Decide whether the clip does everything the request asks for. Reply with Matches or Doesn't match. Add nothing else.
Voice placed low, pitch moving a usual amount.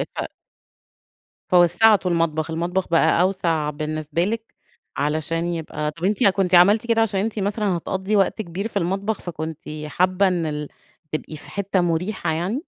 Doesn't match